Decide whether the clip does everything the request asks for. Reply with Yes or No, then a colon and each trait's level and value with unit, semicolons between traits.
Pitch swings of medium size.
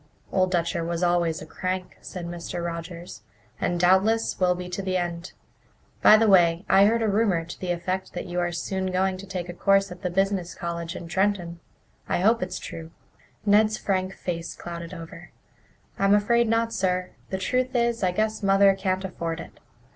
No: narrow, 2.3 semitones